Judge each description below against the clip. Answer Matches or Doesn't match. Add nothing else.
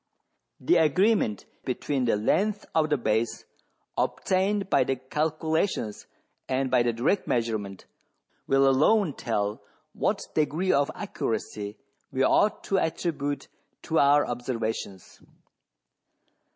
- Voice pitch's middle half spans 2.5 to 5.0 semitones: Doesn't match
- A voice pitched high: Doesn't match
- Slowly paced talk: Matches